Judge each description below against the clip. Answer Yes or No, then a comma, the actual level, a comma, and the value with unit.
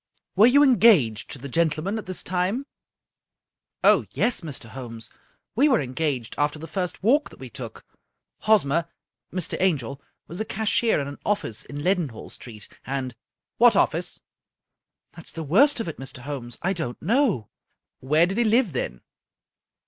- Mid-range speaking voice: Yes, medium, 165 Hz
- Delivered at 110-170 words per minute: No, average, 185 wpm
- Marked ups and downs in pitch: Yes, wide, 7.8 semitones